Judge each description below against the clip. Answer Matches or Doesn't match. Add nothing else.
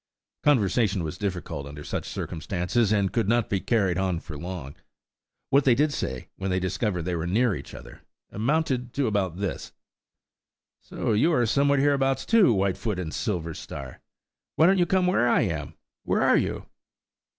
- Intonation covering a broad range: Matches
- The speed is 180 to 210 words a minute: Doesn't match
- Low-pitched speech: Matches